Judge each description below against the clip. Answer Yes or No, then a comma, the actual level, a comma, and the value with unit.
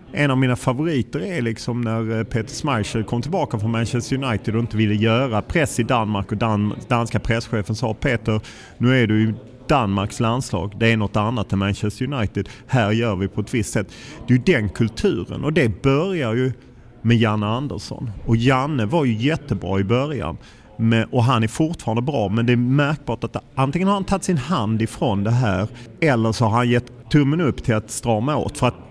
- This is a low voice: Yes, low, 115 Hz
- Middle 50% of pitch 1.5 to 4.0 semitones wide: Yes, average, 2.9 semitones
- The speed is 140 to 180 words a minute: No, fast, 205 wpm